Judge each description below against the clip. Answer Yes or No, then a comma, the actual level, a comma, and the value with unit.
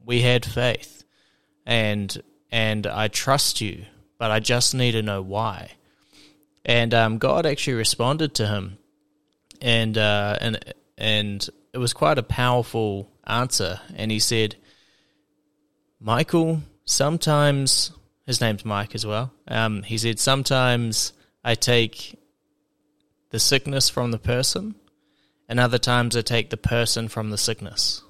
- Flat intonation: No, average, 4.0 semitones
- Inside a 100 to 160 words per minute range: Yes, slow, 135 wpm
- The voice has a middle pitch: No, low, 120 Hz